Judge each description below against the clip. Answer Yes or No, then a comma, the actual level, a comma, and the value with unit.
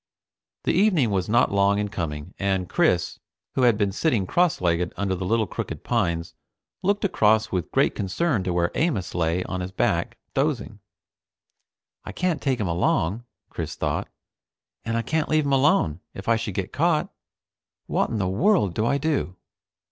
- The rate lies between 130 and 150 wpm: No, average, 175 wpm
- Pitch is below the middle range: Yes, low, 105 Hz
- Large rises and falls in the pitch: Yes, wide, 7.2 semitones